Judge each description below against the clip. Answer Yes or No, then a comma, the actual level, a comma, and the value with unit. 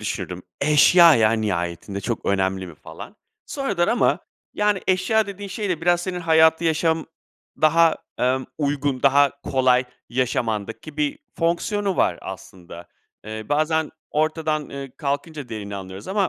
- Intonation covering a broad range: Yes, wide, 7.3 semitones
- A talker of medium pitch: Yes, medium, 145 Hz